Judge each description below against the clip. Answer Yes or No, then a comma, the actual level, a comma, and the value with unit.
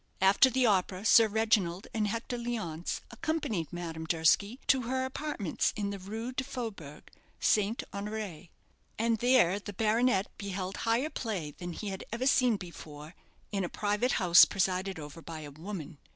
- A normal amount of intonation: Yes, average, 4.7 semitones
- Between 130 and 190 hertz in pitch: No, high, 200 Hz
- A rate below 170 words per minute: Yes, average, 160 wpm